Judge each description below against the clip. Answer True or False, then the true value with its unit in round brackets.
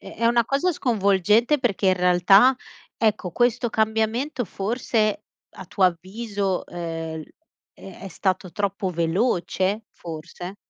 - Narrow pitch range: False (4.4 semitones)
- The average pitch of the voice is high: True (200 Hz)